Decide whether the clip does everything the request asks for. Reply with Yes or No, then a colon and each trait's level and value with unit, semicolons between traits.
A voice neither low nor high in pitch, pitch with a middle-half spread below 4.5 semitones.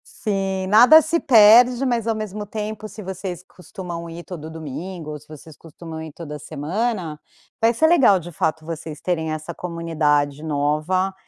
No: medium, 175 Hz; average, 5.2 semitones